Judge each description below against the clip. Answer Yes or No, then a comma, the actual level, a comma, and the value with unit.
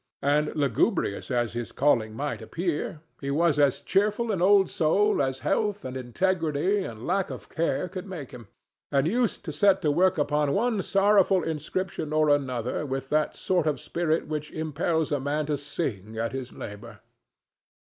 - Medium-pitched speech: Yes, medium, 155 Hz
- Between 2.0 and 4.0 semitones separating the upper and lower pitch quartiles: No, average, 5.3 semitones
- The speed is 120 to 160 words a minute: No, average, 170 wpm